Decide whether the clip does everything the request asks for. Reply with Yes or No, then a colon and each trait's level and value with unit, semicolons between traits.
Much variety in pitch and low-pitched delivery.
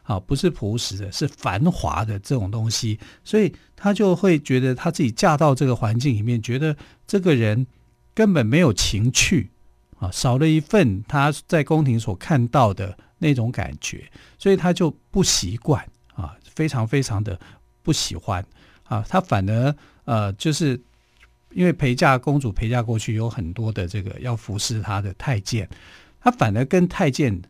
Yes: wide, 6.3 semitones; low, 120 Hz